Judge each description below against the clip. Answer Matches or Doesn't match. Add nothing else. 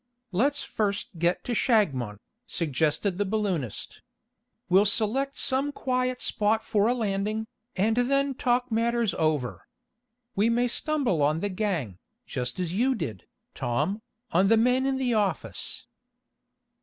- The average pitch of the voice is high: Matches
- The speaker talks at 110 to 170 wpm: Matches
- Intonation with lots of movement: Matches